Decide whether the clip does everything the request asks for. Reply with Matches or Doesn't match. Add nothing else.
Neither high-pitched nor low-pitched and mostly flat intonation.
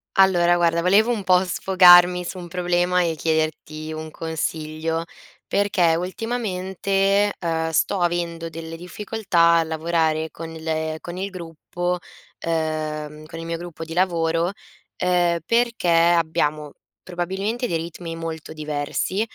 Matches